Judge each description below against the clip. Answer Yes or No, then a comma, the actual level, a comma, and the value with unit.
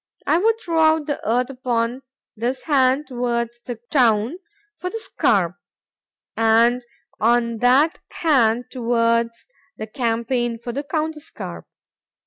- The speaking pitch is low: No, high, 245 Hz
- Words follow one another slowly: Yes, slow, 115 wpm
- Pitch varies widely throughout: No, average, 3.9 semitones